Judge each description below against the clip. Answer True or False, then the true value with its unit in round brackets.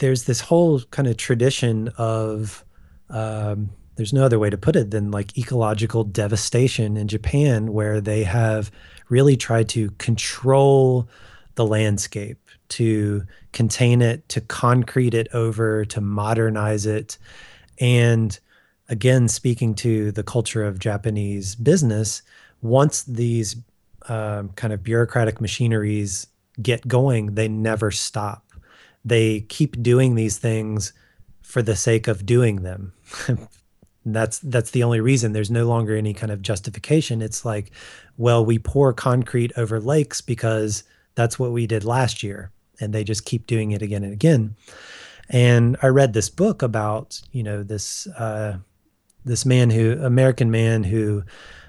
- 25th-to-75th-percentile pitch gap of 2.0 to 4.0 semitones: True (2.4 semitones)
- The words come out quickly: False (145 wpm)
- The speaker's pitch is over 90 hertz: True (110 Hz)